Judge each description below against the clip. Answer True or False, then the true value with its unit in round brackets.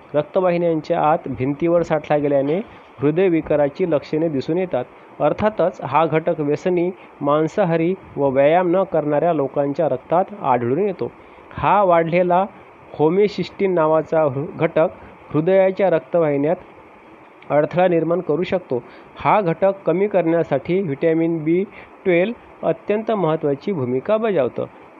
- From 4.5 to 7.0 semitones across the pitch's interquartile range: False (3.6 semitones)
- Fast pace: False (110 wpm)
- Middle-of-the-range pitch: True (165 Hz)